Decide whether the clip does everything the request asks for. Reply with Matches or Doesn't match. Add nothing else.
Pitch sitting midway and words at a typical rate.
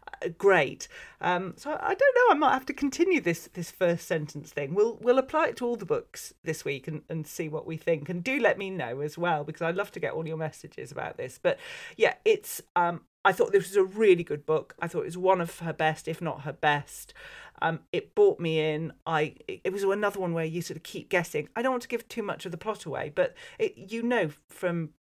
Doesn't match